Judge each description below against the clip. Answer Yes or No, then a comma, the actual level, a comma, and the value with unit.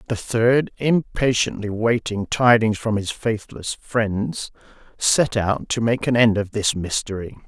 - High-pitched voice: No, low, 110 Hz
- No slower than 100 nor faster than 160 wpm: Yes, average, 145 wpm